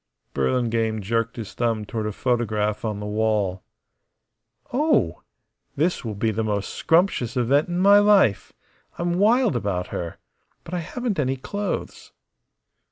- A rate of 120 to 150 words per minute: Yes, average, 140 wpm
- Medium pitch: No, low, 115 Hz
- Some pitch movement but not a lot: No, wide, 8.7 semitones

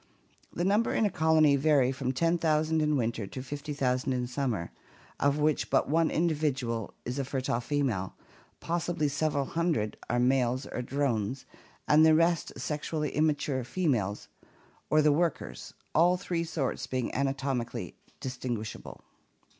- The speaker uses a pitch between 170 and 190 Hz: No, medium, 140 Hz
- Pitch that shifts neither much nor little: Yes, average, 3.8 semitones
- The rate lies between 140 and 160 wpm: Yes, average, 145 wpm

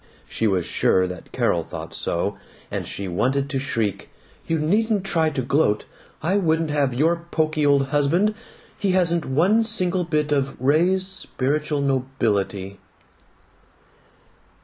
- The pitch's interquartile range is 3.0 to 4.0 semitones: No, average, 4.8 semitones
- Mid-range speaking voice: Yes, medium, 150 Hz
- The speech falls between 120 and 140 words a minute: Yes, slow, 135 wpm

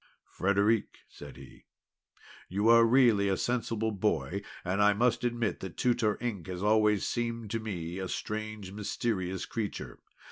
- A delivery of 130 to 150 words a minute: Yes, average, 145 wpm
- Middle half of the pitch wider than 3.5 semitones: No, average, 3.1 semitones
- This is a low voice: Yes, low, 105 Hz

